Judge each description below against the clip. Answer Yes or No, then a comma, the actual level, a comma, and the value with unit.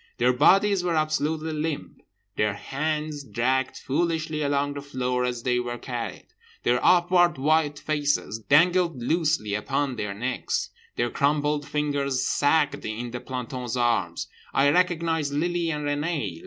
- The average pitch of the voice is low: No, medium, 145 Hz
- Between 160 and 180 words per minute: No, average, 140 wpm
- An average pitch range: Yes, average, 4.1 semitones